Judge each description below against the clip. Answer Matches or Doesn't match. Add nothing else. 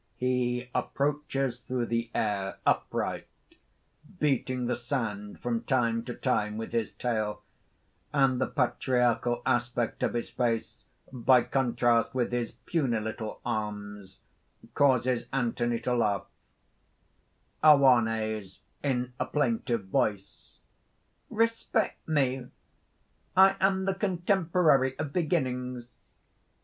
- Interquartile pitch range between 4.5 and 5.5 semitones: Doesn't match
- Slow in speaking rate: Matches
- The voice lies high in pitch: Doesn't match